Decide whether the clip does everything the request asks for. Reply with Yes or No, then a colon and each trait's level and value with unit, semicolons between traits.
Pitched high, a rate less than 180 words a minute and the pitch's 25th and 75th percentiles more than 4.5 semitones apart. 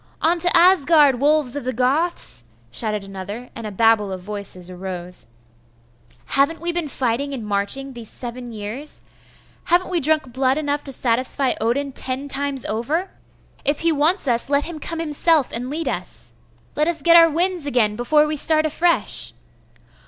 Yes: very high, 275 Hz; average, 165 wpm; average, 5.2 semitones